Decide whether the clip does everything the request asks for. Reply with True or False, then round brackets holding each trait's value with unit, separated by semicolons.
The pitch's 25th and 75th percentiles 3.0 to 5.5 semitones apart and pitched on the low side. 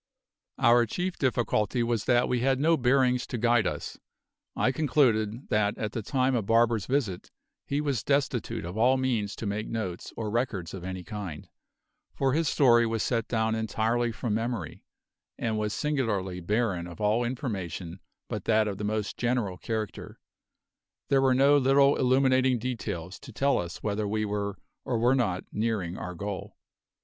True (3.7 semitones; 115 Hz)